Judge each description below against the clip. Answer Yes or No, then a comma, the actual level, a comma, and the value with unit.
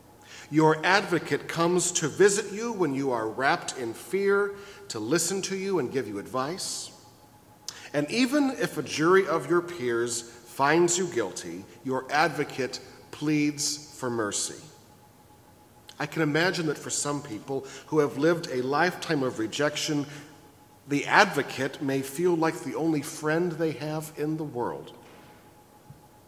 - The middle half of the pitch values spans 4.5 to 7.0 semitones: Yes, average, 5.1 semitones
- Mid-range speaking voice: Yes, medium, 145 Hz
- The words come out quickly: No, average, 145 wpm